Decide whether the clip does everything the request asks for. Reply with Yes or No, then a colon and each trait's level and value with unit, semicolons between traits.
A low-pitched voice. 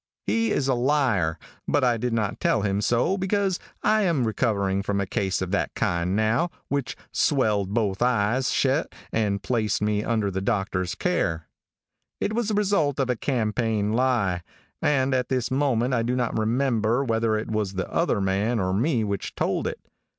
Yes: low, 115 Hz